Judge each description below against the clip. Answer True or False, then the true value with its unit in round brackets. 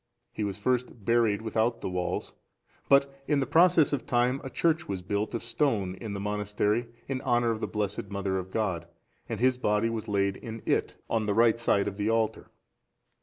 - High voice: False (110 Hz)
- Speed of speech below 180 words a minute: False (200 wpm)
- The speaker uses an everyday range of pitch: True (3.3 semitones)